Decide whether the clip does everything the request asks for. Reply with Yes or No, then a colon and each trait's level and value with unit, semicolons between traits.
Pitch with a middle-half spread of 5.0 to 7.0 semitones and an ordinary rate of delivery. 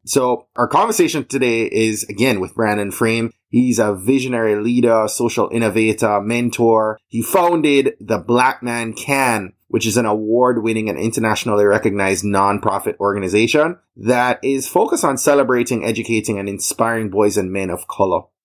No: average, 2.8 semitones; average, 145 wpm